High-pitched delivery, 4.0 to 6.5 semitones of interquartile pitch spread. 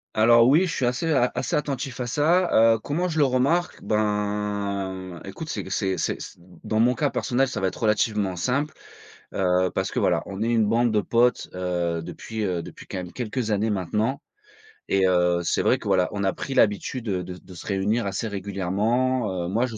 No: low, 110 Hz; average, 4.6 semitones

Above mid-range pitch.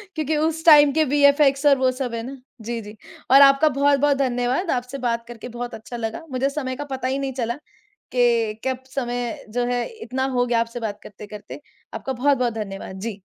Yes: very high, 255 Hz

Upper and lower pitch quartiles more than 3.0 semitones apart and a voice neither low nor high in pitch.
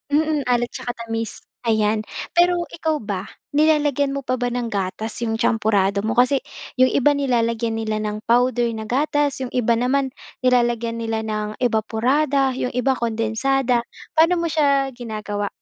No: average, 3.6 semitones; high, 240 Hz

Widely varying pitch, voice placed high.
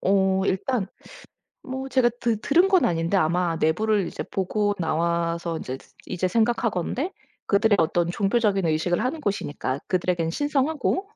Yes: wide, 6.0 semitones; high, 195 Hz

